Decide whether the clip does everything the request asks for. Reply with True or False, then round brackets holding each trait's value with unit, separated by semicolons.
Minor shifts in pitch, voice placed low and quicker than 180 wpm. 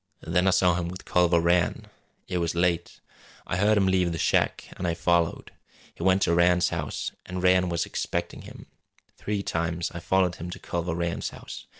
True (1.3 semitones; 90 Hz; 195 wpm)